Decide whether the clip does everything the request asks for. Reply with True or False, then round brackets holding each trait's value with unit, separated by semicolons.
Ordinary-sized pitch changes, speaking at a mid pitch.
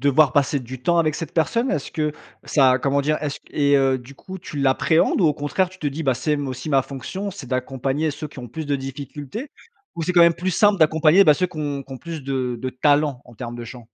True (3.3 semitones; 145 Hz)